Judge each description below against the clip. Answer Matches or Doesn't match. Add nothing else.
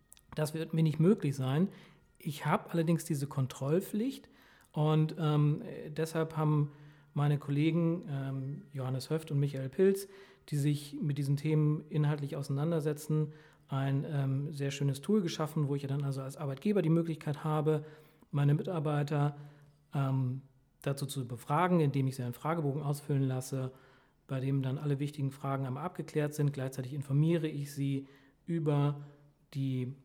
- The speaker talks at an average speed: Matches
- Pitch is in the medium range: Matches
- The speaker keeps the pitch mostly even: Matches